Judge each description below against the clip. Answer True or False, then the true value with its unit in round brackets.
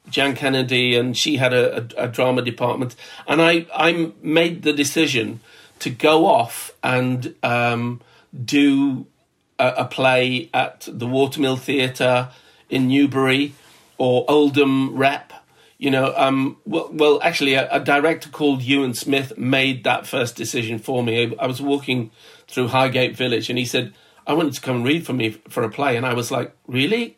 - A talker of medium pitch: False (130 Hz)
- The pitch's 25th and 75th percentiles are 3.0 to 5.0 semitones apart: False (2.4 semitones)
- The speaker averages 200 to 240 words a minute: False (170 wpm)